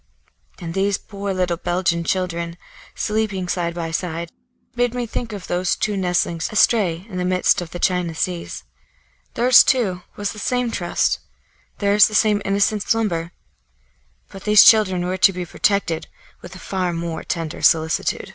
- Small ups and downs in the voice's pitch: No, average, 3.3 semitones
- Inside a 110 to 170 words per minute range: Yes, average, 160 wpm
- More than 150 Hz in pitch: Yes, medium, 185 Hz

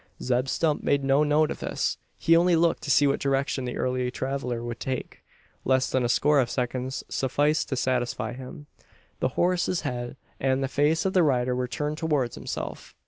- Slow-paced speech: No, average, 195 wpm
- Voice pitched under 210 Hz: Yes, low, 135 Hz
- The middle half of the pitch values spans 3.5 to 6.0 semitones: No, average, 2.9 semitones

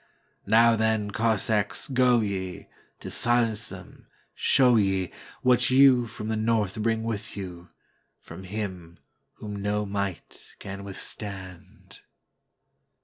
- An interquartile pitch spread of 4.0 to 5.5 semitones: No, average, 2.7 semitones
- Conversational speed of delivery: No, slow, 100 wpm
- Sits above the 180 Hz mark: No, low, 105 Hz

